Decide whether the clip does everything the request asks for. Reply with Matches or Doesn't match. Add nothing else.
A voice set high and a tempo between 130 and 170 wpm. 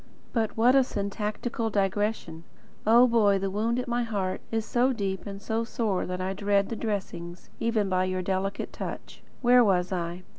Doesn't match